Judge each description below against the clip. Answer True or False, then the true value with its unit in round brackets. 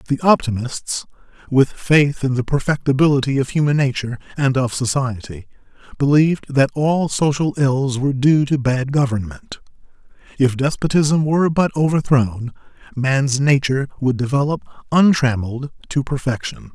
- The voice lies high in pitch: False (135 Hz)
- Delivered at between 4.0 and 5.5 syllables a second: True (5.0 syllables/s)